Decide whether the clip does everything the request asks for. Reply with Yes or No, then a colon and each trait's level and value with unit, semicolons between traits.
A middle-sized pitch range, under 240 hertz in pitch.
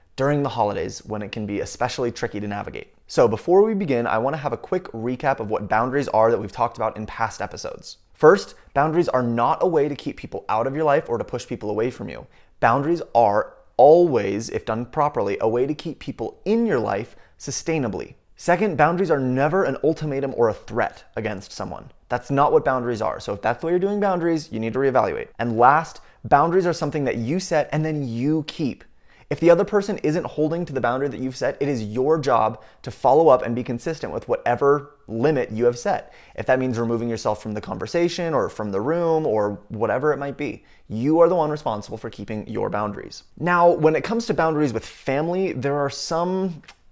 No: wide, 5.9 semitones; medium, 140 Hz